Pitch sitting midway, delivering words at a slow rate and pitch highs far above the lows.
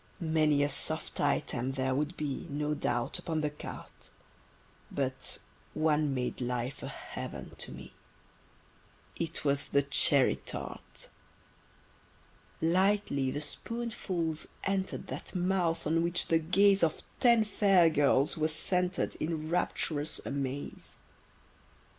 No: medium, 155 Hz; slow, 120 wpm; average, 3.9 semitones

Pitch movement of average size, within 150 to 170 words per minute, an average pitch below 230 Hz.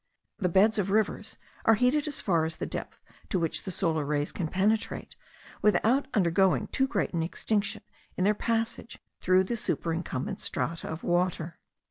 Yes: average, 4.7 semitones; average, 165 wpm; high, 190 Hz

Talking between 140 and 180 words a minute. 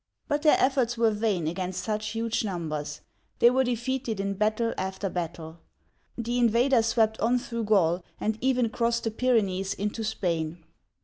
Yes: average, 160 wpm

